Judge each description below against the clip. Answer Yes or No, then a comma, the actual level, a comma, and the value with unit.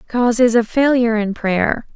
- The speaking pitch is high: Yes, high, 230 Hz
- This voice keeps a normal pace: Yes, average, 155 wpm